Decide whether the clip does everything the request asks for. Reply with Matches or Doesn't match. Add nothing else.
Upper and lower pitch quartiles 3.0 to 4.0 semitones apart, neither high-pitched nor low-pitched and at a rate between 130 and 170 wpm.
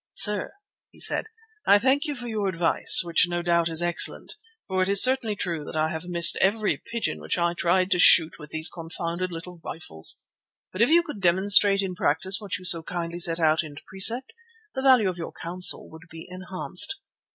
Doesn't match